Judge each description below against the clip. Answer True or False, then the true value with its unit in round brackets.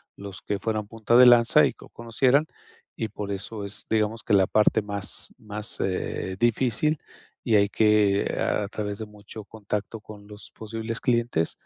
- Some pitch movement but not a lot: False (1.9 semitones)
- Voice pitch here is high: False (105 Hz)